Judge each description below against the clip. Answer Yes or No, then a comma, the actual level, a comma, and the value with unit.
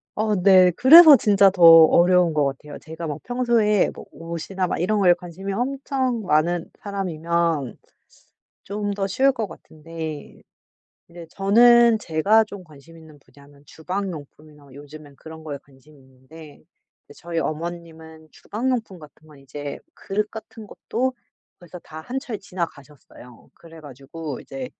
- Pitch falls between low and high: Yes, medium, 170 Hz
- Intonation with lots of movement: No, average, 5.0 semitones